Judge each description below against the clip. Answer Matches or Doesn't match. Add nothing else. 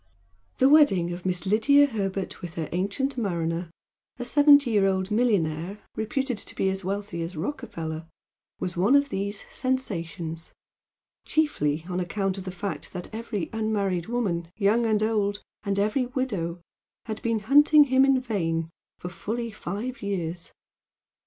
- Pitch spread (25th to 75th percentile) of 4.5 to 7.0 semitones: Matches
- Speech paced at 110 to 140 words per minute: Doesn't match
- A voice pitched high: Matches